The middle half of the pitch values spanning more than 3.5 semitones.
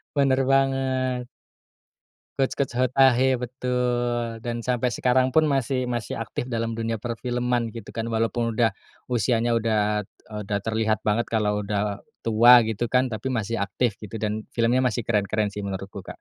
No: narrow, 2.5 semitones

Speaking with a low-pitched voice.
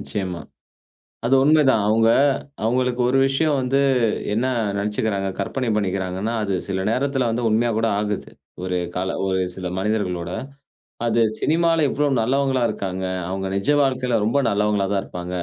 Yes: low, 110 Hz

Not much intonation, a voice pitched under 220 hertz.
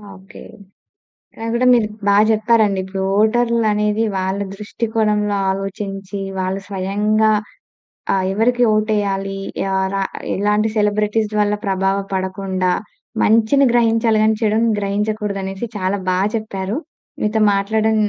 Yes: narrow, 2.0 semitones; high, 210 Hz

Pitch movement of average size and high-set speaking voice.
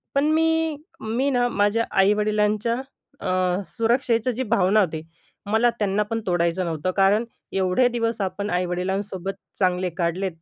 Yes: average, 3.8 semitones; high, 205 Hz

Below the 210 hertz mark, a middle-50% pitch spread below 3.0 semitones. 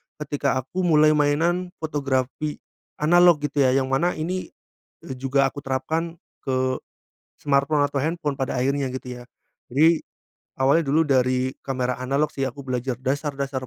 Yes: medium, 140 Hz; narrow, 2.6 semitones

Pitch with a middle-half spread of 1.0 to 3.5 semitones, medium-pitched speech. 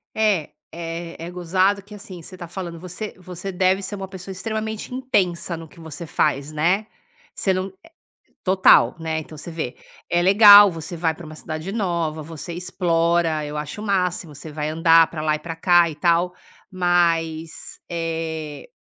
Yes: average, 2.7 semitones; medium, 170 Hz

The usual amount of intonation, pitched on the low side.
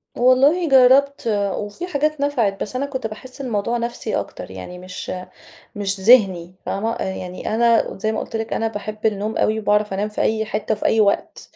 No: average, 3.8 semitones; high, 220 Hz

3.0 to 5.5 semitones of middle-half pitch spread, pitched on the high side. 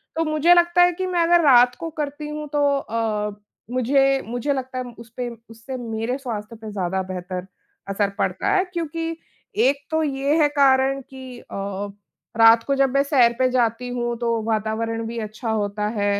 Yes: average, 4.2 semitones; very high, 250 Hz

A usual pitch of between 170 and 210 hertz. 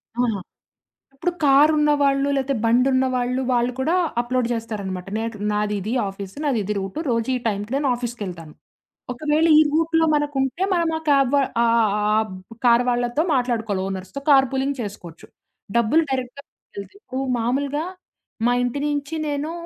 No: very high, 250 Hz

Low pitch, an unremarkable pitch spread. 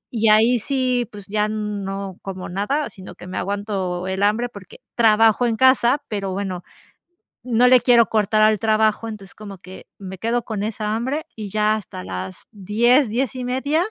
No: high, 215 Hz; average, 3.3 semitones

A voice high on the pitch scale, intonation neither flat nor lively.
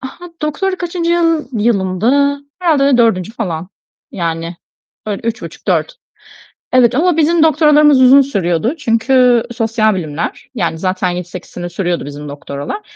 No: high, 230 Hz; wide, 8.5 semitones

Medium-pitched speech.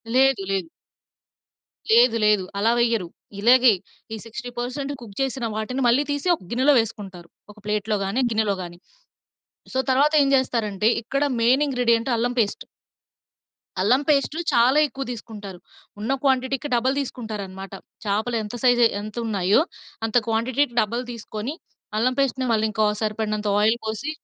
No: high, 230 Hz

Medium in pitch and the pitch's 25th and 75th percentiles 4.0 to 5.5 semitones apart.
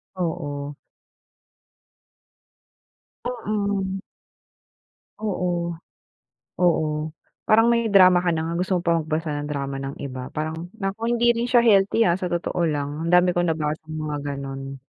Yes: medium, 170 Hz; average, 4.4 semitones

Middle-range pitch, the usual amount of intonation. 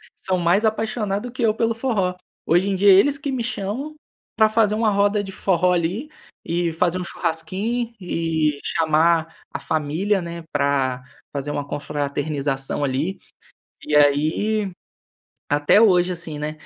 No: medium, 180 Hz; wide, 5.7 semitones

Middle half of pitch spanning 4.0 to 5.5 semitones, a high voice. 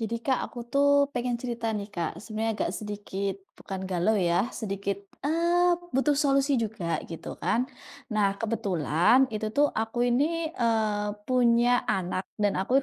Yes: average, 4.3 semitones; high, 225 Hz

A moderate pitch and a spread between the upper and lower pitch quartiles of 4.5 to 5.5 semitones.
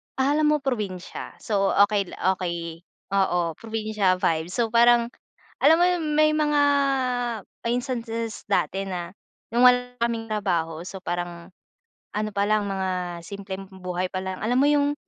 No: high, 200 Hz; average, 4.8 semitones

